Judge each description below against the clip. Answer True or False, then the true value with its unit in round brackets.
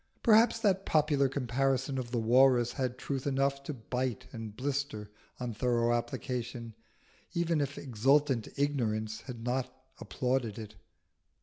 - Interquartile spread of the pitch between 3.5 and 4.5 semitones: False (3.0 semitones)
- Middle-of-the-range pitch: False (130 Hz)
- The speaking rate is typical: False (130 wpm)